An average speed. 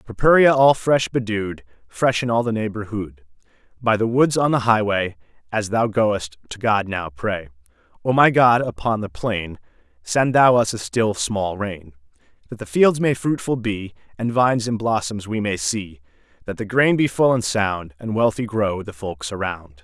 Yes: average, 180 wpm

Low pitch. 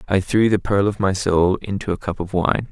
Yes: very low, 95 Hz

